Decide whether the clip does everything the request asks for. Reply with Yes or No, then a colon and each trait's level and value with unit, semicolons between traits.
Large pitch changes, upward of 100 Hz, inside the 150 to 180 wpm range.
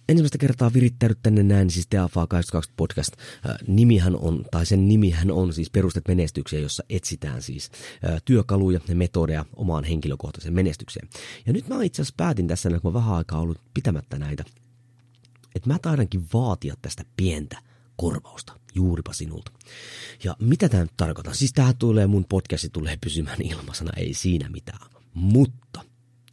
No: wide, 6.2 semitones; very low, 95 Hz; fast, 155 wpm